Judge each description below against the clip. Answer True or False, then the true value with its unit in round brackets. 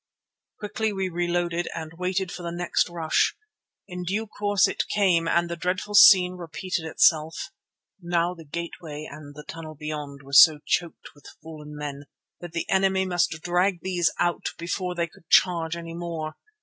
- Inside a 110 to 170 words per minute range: True (165 wpm)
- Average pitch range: False (2.3 semitones)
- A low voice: False (170 Hz)